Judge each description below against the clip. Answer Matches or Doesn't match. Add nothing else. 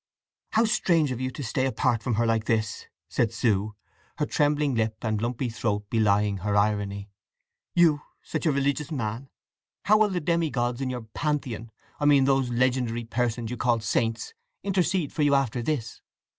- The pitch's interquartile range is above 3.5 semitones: Matches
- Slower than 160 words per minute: Doesn't match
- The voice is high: Doesn't match